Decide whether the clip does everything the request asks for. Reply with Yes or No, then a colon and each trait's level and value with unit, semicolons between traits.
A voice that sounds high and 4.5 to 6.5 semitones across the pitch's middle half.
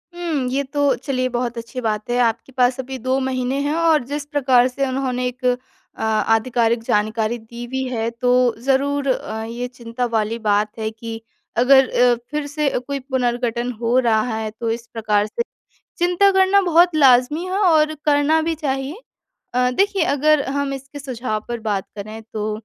No: very high, 250 Hz; average, 3.6 semitones